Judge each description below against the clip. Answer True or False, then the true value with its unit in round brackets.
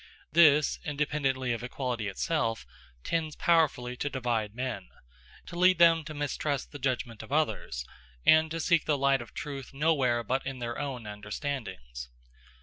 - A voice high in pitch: False (135 Hz)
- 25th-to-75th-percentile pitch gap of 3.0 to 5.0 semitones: True (4.3 semitones)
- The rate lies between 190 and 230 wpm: False (150 wpm)